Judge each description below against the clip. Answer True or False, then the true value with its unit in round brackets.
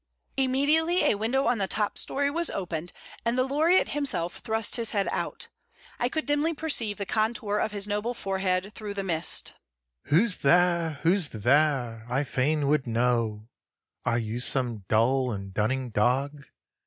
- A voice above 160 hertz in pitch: True (185 Hz)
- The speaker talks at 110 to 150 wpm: False (160 wpm)